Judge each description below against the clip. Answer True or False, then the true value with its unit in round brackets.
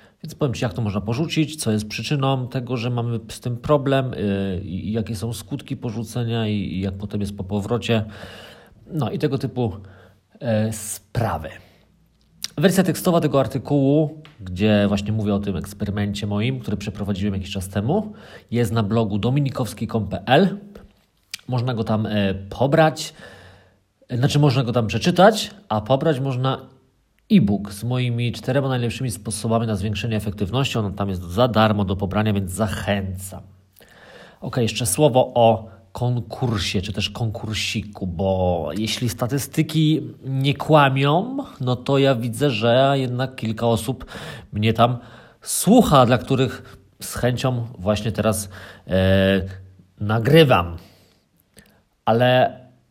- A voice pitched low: True (115 Hz)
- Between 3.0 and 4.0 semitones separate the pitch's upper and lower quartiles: False (4.7 semitones)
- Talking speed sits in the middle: True (135 wpm)